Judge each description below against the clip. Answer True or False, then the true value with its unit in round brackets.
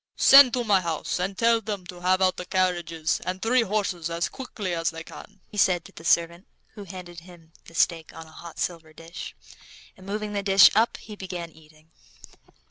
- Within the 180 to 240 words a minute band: True (205 wpm)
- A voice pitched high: False (180 Hz)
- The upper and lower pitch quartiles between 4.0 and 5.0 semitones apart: False (3.3 semitones)